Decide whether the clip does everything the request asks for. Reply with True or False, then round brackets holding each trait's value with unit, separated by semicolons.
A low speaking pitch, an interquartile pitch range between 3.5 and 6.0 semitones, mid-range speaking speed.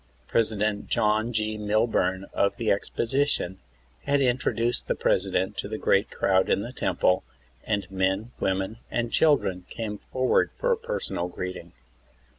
True (105 Hz; 3.8 semitones; 145 wpm)